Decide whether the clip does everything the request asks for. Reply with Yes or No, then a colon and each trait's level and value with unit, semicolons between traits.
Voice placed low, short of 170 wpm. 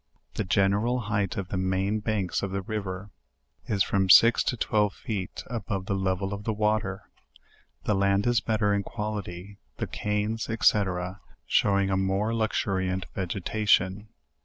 Yes: low, 100 Hz; average, 150 wpm